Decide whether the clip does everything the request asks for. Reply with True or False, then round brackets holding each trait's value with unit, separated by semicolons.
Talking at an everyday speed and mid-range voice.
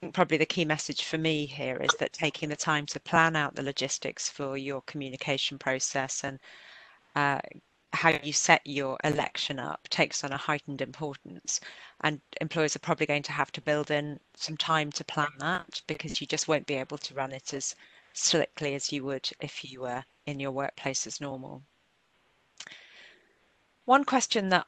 True (180 wpm; 150 Hz)